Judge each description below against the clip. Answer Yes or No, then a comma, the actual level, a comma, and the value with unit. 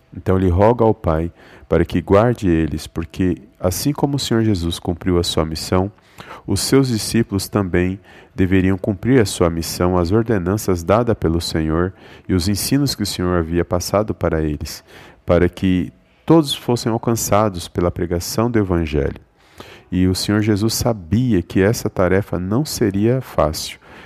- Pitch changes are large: No, average, 4.2 semitones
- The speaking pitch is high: No, very low, 95 Hz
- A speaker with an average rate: Yes, average, 155 wpm